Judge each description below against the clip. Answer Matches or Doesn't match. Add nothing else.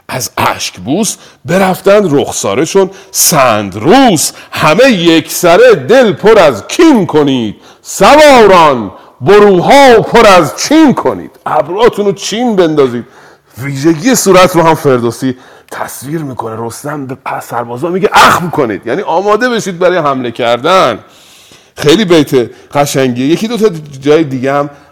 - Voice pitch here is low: Doesn't match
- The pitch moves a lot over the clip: Matches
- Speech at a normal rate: Matches